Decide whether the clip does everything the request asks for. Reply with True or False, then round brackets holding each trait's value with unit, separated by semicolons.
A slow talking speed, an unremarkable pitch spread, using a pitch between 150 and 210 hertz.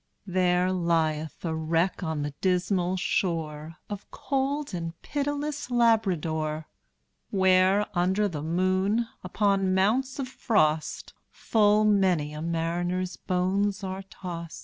True (115 wpm; 3.7 semitones; 185 Hz)